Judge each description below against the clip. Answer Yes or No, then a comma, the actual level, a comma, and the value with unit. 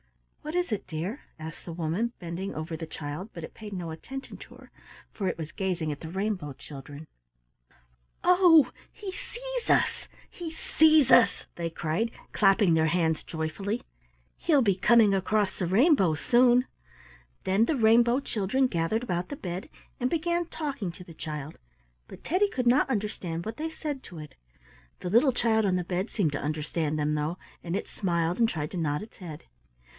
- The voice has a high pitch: Yes, high, 195 Hz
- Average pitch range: No, wide, 7.1 semitones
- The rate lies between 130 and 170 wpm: No, average, 180 wpm